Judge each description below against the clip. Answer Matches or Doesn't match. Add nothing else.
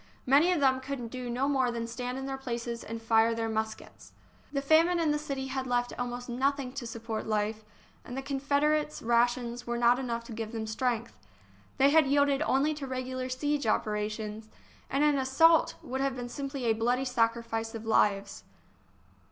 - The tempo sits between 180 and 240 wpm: Matches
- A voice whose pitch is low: Doesn't match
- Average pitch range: Matches